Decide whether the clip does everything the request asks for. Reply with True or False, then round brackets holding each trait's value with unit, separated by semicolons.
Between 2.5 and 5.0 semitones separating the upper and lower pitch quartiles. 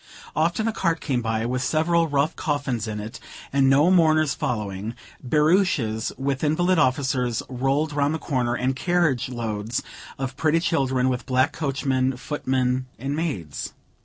True (3.9 semitones)